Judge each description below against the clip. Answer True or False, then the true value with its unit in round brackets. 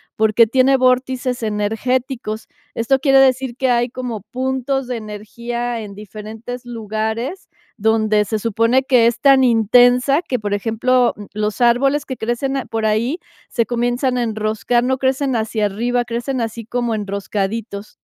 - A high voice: True (240 Hz)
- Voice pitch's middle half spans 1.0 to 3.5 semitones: True (2.8 semitones)